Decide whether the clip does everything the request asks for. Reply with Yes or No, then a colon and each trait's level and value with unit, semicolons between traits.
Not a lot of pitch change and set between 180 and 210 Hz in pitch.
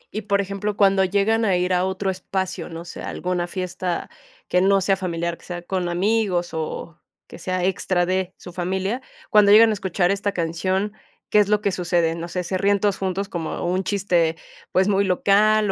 Yes: narrow, 2.1 semitones; high, 190 Hz